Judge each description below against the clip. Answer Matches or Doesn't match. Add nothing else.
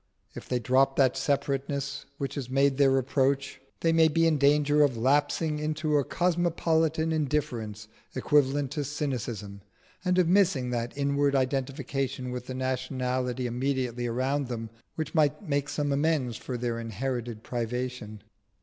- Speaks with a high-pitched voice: Doesn't match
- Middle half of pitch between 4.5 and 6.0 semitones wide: Doesn't match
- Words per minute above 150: Doesn't match